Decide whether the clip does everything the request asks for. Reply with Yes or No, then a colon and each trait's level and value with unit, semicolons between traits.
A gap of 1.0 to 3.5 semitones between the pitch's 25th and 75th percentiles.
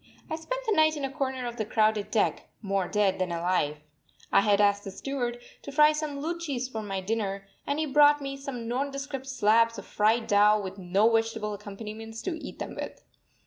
No: average, 5.3 semitones